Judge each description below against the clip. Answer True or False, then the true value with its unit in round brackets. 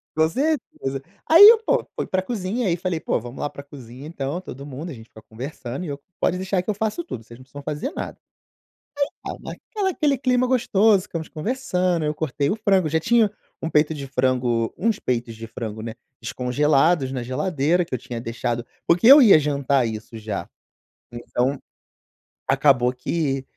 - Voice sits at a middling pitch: True (150 Hz)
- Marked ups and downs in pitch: True (7.0 semitones)